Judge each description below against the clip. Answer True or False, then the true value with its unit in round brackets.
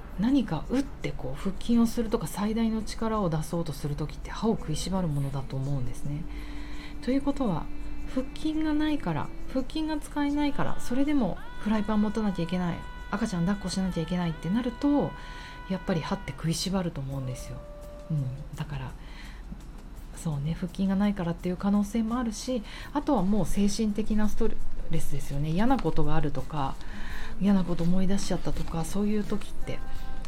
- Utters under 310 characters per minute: False (390 characters per minute)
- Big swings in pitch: True (6.4 semitones)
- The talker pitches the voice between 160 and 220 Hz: True (185 Hz)